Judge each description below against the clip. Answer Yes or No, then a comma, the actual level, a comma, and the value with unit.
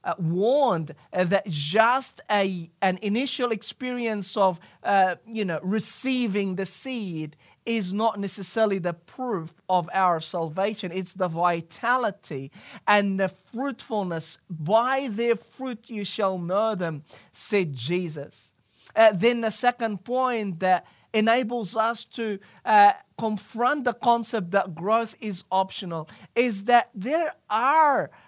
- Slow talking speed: Yes, slow, 125 wpm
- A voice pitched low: No, high, 205 Hz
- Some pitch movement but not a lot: Yes, average, 4.2 semitones